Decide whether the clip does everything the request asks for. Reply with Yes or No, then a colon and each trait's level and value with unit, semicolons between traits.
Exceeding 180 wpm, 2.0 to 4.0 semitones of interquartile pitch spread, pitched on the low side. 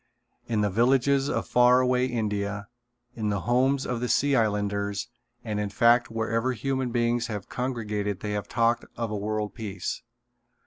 No: average, 165 wpm; average, 3.1 semitones; low, 115 Hz